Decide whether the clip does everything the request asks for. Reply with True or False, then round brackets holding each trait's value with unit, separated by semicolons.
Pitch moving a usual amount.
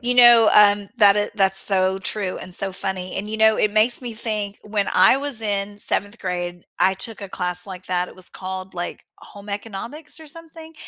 True (3.0 semitones)